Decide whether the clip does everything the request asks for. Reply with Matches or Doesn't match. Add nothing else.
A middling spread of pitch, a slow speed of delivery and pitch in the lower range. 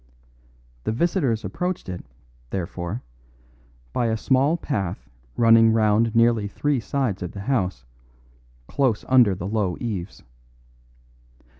Matches